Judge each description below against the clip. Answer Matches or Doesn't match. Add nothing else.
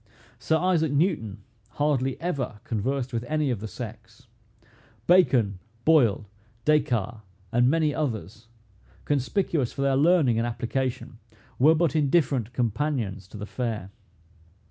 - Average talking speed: Doesn't match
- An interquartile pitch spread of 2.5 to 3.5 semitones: Doesn't match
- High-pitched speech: Doesn't match